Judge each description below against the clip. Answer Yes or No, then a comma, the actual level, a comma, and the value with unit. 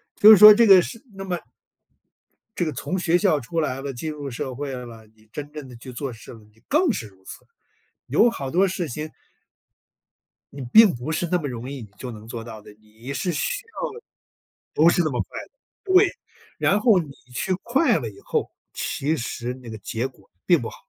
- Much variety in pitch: Yes, wide, 7.2 semitones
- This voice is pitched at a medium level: Yes, medium, 145 Hz